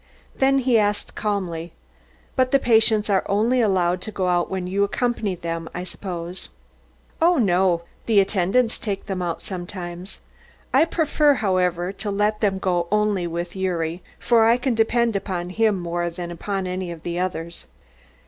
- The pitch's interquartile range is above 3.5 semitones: Yes, average, 3.9 semitones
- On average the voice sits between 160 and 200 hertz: Yes, high, 190 Hz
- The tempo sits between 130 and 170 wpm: Yes, average, 165 wpm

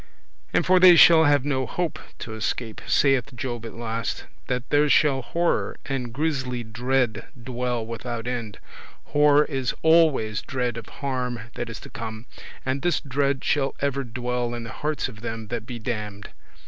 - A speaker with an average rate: Yes, average, 170 wpm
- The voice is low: Yes, low, 125 Hz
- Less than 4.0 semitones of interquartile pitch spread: Yes, average, 3.3 semitones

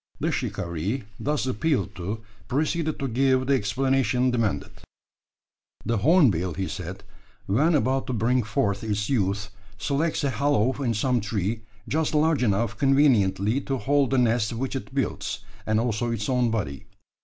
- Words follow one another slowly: No, average, 155 wpm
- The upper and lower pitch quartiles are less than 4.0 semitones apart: No, average, 4.6 semitones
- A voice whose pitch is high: No, low, 120 Hz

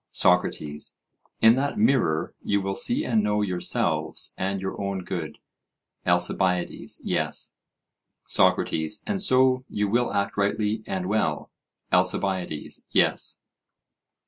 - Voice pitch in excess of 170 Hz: No, low, 100 Hz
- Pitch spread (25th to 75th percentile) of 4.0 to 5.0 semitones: No, average, 3.6 semitones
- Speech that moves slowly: Yes, slow, 115 wpm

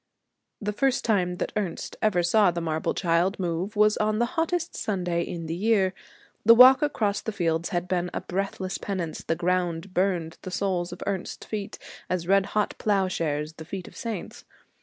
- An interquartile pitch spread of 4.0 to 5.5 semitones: No, average, 3.4 semitones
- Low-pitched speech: No, medium, 185 Hz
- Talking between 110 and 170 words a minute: No, average, 185 wpm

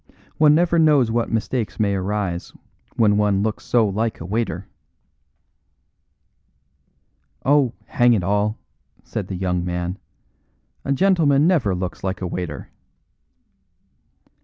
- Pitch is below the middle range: Yes, low, 105 Hz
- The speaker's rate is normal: No, slow, 120 wpm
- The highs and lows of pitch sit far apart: Yes, wide, 5.7 semitones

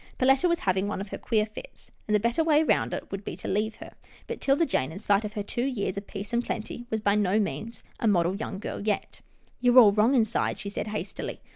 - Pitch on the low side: No, high, 215 Hz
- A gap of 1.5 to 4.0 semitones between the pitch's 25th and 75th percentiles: Yes, average, 3.1 semitones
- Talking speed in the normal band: No, fast, 245 wpm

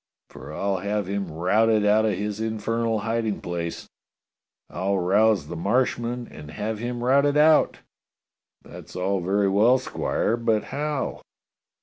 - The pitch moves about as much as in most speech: Yes, average, 3.1 semitones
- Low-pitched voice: Yes, low, 105 Hz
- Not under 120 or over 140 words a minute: Yes, slow, 135 wpm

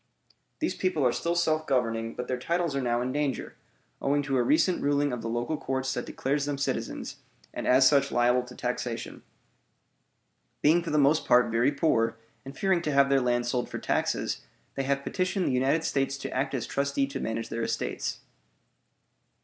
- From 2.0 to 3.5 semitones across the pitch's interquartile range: Yes, average, 3.0 semitones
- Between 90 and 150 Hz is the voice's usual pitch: Yes, low, 135 Hz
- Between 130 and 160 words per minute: No, average, 190 wpm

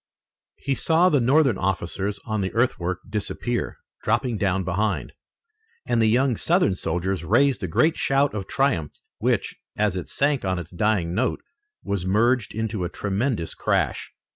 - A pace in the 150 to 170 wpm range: Yes, average, 155 wpm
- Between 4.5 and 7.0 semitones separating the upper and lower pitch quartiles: Yes, wide, 5.4 semitones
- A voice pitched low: Yes, low, 105 Hz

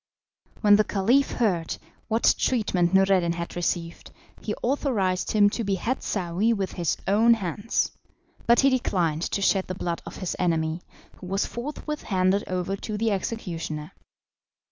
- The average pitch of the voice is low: No, high, 195 Hz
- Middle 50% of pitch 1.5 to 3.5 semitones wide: No, average, 4.2 semitones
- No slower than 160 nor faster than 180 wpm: No, average, 150 wpm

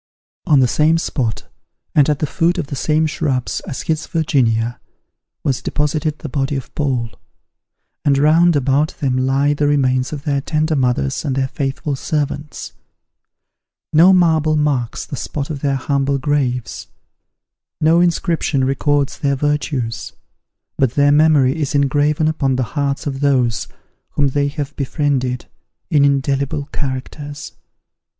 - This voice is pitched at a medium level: Yes, medium, 145 Hz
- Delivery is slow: No, average, 145 wpm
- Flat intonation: Yes, narrow, 2.3 semitones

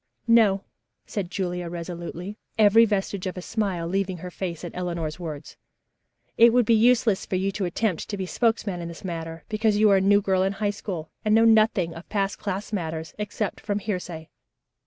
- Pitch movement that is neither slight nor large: Yes, average, 3.3 semitones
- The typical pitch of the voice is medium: No, high, 195 Hz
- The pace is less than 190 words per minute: No, average, 195 wpm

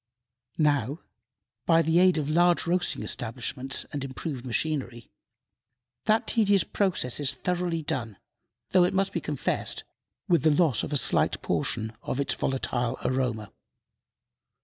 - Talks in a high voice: No, medium, 145 Hz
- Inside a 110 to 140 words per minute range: Yes, slow, 135 wpm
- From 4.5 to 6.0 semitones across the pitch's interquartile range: Yes, wide, 5.5 semitones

